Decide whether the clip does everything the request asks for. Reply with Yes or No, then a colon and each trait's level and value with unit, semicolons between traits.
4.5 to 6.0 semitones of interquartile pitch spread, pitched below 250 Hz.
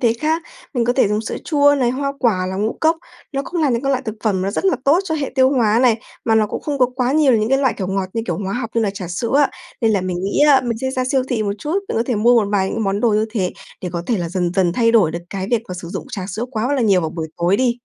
Yes: average, 5.0 semitones; high, 230 Hz